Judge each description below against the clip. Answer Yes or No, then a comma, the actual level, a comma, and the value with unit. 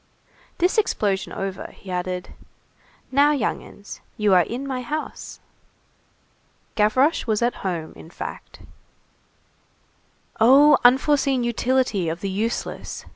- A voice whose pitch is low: No, high, 230 Hz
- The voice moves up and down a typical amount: No, wide, 5.7 semitones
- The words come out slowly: Yes, slow, 115 wpm